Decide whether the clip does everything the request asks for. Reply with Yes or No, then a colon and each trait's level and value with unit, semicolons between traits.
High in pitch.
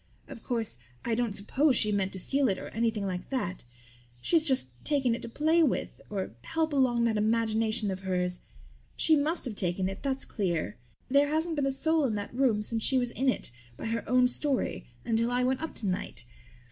Yes: high, 235 Hz